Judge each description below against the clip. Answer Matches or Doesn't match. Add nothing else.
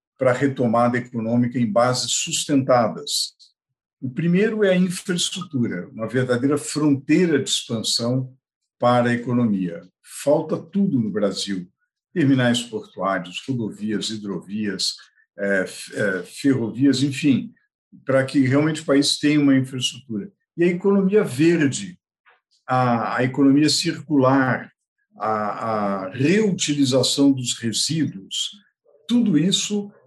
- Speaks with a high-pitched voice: Doesn't match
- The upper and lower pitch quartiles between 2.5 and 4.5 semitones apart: Doesn't match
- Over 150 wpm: Doesn't match